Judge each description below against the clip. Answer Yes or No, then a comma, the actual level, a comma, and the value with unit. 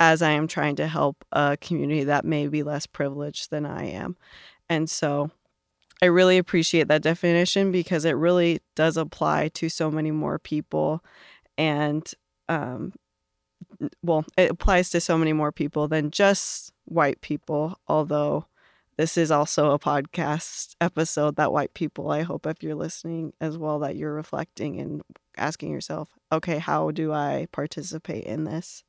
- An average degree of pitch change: No, narrow, 1.9 semitones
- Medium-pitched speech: Yes, medium, 155 Hz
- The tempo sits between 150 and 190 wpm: Yes, average, 160 wpm